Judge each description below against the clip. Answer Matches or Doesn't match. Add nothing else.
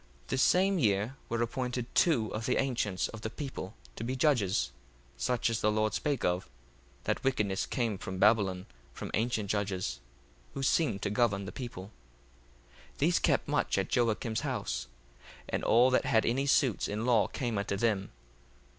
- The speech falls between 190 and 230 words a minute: Doesn't match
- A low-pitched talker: Matches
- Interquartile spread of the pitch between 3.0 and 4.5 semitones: Matches